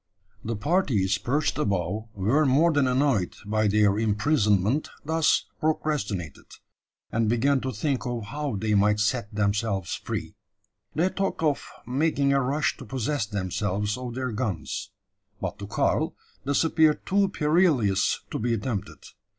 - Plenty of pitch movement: Yes, wide, 5.9 semitones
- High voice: No, low, 115 Hz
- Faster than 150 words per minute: No, average, 140 wpm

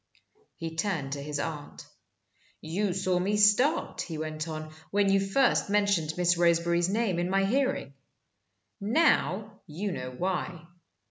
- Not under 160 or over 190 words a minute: No, average, 140 wpm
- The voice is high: No, medium, 180 Hz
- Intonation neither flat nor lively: Yes, average, 4.2 semitones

